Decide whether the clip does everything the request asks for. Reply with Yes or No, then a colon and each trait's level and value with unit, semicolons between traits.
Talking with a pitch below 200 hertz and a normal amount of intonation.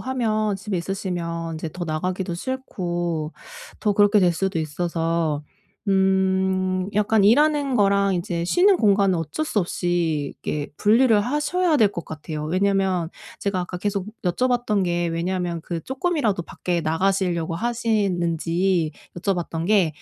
Yes: medium, 185 Hz; average, 3.6 semitones